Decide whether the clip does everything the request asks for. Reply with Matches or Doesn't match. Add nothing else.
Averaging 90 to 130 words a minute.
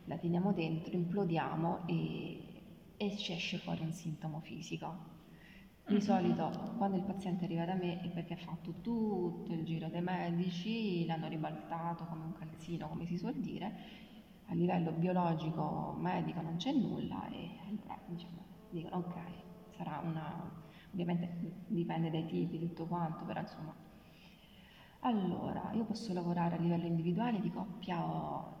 Doesn't match